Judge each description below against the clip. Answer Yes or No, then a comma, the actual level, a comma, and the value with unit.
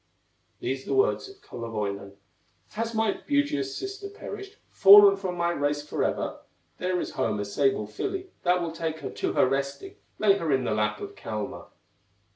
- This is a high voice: No, medium, 165 Hz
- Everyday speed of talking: Yes, average, 170 wpm